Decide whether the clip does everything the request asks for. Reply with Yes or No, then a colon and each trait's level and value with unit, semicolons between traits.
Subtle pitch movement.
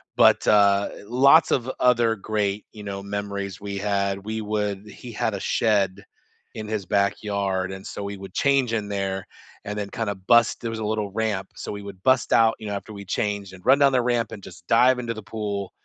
Yes: narrow, 2.2 semitones